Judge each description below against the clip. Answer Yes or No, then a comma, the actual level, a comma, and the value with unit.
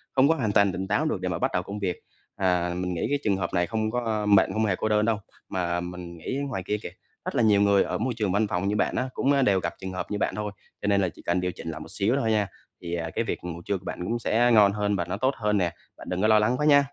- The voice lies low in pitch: Yes, low, 100 Hz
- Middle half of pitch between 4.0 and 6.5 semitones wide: No, average, 3.4 semitones